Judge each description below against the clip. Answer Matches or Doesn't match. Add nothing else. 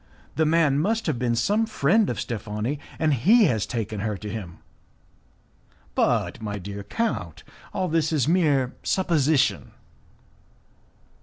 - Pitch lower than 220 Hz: Matches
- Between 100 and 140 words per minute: Matches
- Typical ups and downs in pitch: Doesn't match